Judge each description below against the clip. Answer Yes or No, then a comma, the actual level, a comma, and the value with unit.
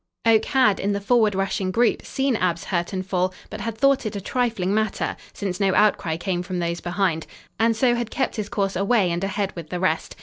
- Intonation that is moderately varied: Yes, average, 3.5 semitones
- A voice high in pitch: Yes, high, 200 Hz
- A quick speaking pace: Yes, fast, 225 wpm